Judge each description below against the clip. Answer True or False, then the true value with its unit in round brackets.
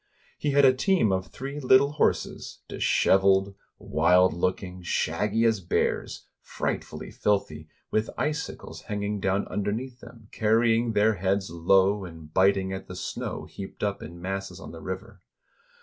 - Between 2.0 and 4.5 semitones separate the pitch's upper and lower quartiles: True (3.3 semitones)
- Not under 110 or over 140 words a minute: False (150 wpm)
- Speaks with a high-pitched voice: False (100 Hz)